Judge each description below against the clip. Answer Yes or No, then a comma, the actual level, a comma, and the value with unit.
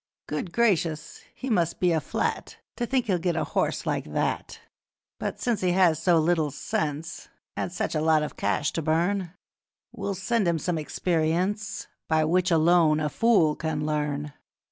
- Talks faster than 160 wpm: Yes, average, 170 wpm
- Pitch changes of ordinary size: Yes, average, 3.1 semitones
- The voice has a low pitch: No, medium, 170 Hz